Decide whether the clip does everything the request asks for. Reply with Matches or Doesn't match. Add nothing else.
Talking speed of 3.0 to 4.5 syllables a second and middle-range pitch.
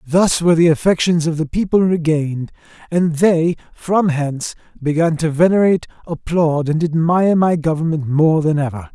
Doesn't match